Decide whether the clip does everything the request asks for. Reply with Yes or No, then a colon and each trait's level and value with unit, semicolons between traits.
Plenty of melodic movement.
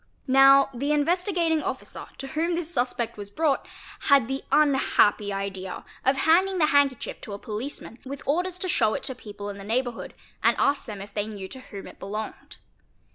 Yes: wide, 6.4 semitones